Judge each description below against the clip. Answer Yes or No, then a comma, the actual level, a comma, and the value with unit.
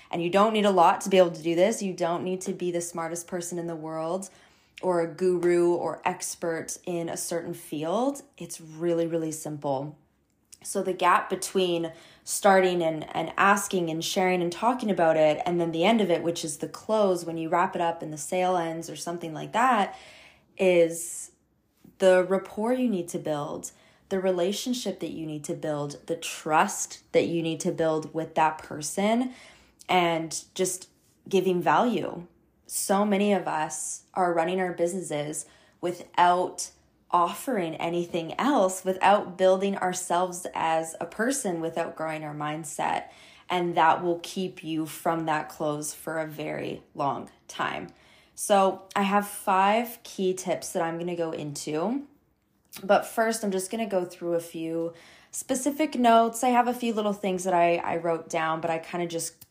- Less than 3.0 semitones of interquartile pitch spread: Yes, narrow, 2.5 semitones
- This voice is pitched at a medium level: Yes, medium, 175 Hz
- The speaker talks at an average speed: Yes, average, 175 wpm